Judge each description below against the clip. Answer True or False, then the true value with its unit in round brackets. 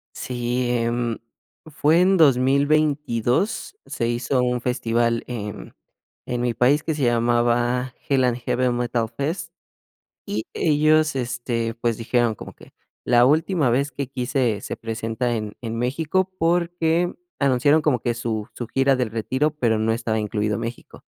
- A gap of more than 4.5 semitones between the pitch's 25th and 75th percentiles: False (3.6 semitones)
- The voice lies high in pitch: False (125 Hz)